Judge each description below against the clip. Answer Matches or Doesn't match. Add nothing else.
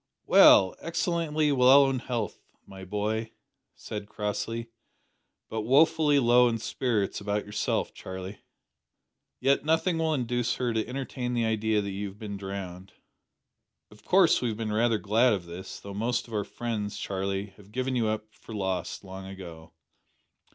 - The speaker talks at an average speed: Matches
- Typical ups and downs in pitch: Matches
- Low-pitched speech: Matches